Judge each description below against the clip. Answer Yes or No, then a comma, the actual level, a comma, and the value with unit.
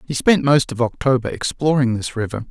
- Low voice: Yes, low, 130 Hz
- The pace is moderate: Yes, average, 190 wpm